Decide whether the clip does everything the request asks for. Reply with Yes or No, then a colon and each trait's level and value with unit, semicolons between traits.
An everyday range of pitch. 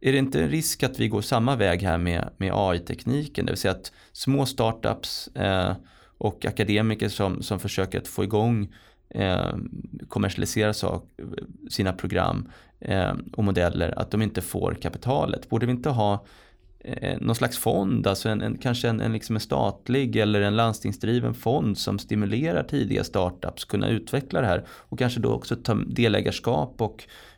Yes: average, 3.6 semitones